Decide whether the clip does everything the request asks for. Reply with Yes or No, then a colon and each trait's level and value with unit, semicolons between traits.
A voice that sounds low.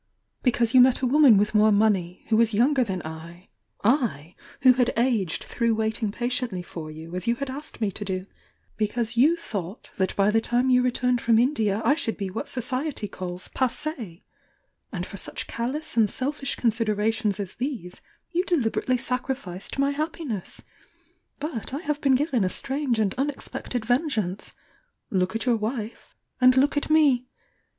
No: high, 235 Hz